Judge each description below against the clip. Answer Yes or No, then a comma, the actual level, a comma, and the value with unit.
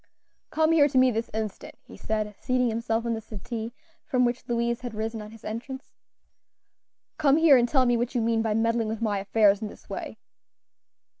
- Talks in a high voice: Yes, high, 230 Hz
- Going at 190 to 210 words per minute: Yes, average, 200 wpm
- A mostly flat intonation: Yes, narrow, 2.3 semitones